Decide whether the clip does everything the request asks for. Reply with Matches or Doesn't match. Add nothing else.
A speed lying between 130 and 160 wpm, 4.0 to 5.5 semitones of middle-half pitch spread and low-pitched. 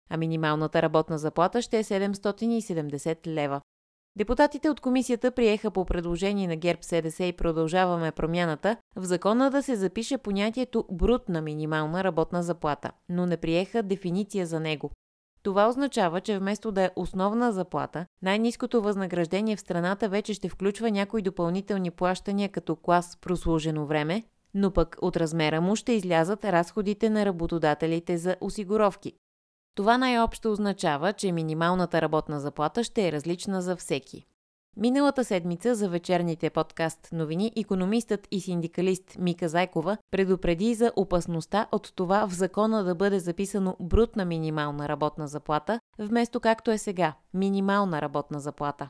Doesn't match